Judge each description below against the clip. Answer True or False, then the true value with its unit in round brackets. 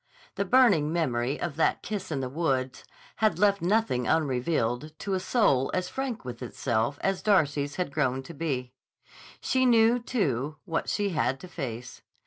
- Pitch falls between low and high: True (155 Hz)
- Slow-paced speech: False (165 wpm)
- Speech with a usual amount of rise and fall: False (7.2 semitones)